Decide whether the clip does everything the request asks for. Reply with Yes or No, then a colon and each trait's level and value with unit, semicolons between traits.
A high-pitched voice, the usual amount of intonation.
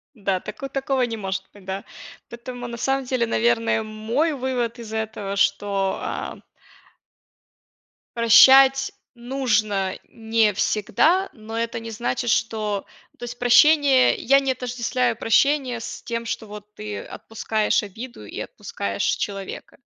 Yes: high, 230 Hz; average, 3.2 semitones